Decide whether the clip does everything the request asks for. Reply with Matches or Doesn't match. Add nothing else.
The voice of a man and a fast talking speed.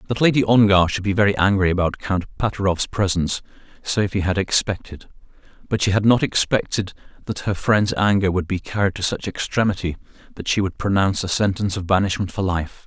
Doesn't match